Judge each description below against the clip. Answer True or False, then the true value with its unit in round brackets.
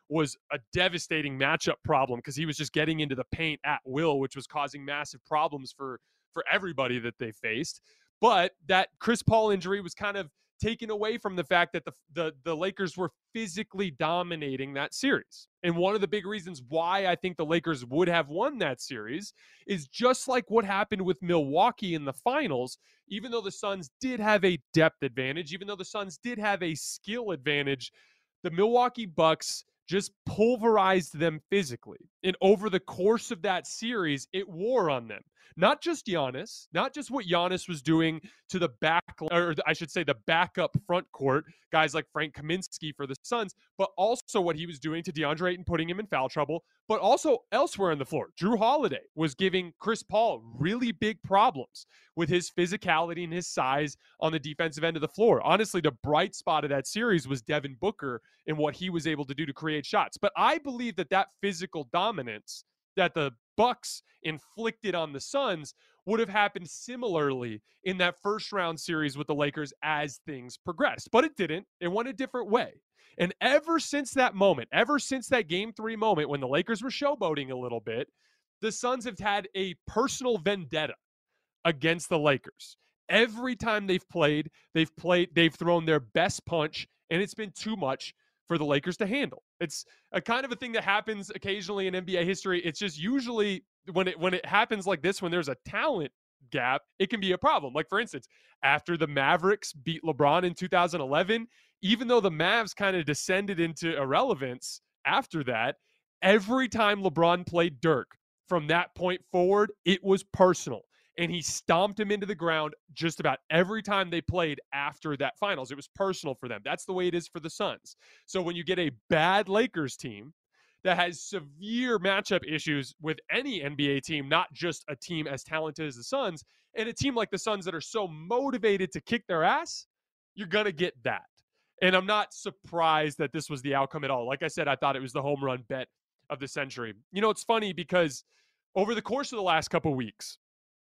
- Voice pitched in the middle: True (175 Hz)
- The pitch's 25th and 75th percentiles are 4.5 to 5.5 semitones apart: True (5.0 semitones)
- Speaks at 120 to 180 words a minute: False (200 wpm)